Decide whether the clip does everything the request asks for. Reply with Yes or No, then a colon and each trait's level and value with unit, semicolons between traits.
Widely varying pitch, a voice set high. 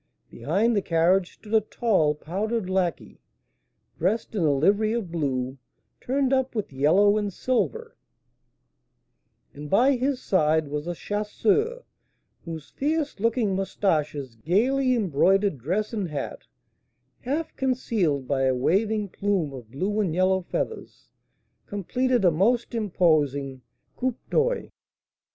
Yes: wide, 7.0 semitones; high, 195 Hz